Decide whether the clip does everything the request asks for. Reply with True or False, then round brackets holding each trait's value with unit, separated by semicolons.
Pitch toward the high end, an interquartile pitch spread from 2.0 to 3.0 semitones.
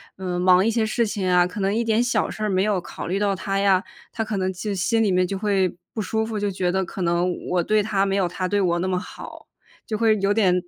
True (195 Hz; 2.7 semitones)